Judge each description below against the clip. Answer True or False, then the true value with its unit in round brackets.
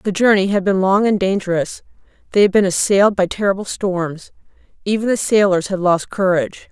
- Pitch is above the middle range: True (195 Hz)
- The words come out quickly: False (180 wpm)